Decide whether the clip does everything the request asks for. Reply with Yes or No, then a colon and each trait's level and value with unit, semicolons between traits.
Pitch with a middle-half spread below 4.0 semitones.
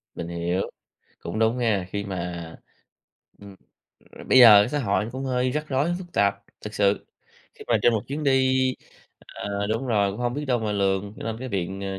No: average, 4.5 semitones